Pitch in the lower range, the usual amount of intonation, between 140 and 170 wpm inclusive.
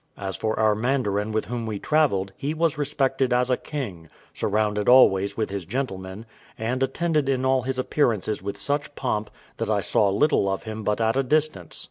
No: low, 115 Hz; average, 4.9 semitones; average, 190 wpm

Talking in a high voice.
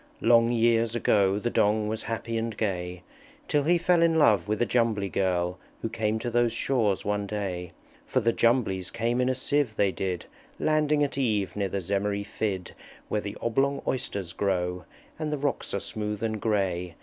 No: low, 110 Hz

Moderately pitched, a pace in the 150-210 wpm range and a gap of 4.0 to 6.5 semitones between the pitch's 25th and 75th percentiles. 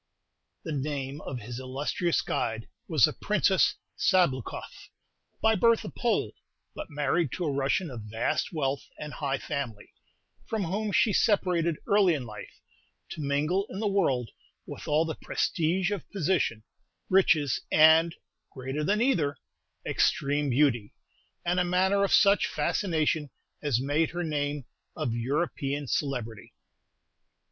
No: medium, 150 Hz; slow, 135 wpm; average, 5.0 semitones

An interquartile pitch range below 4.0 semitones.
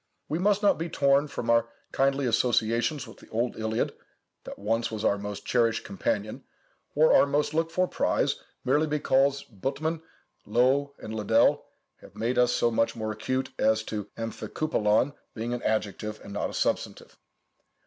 No: average, 4.5 semitones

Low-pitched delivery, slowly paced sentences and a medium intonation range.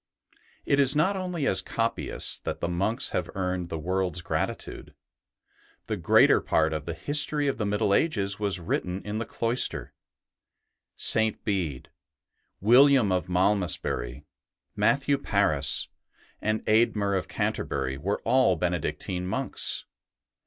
Yes: low, 100 Hz; slow, 130 wpm; average, 4.8 semitones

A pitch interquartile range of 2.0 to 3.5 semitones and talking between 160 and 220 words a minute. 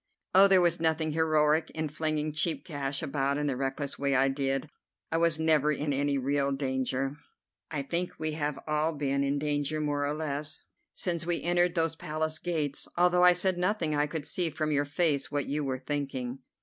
Yes: narrow, 2.4 semitones; average, 195 wpm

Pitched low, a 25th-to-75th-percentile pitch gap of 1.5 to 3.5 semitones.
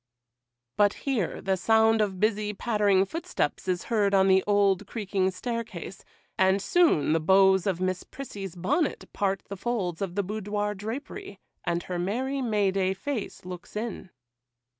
No: high, 200 Hz; average, 2.8 semitones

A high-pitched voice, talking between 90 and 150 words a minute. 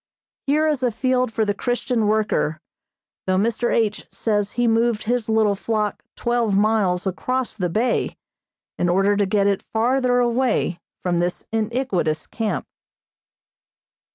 Yes: high, 220 Hz; average, 140 wpm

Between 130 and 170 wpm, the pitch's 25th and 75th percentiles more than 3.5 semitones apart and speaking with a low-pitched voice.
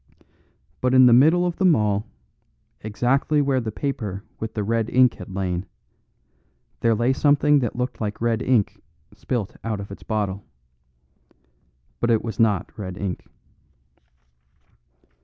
Yes: average, 140 wpm; average, 3.9 semitones; low, 115 Hz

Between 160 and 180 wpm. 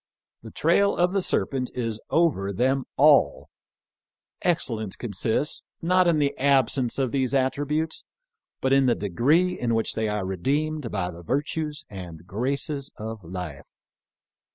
No: average, 150 wpm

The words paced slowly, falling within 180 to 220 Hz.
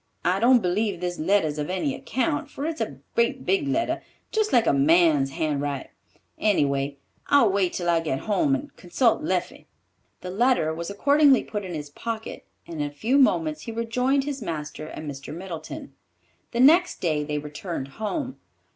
No: average, 180 wpm; high, 190 Hz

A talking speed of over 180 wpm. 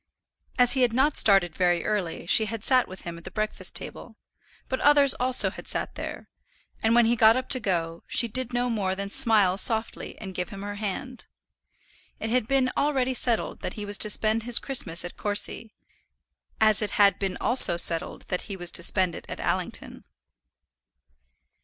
Yes: average, 190 wpm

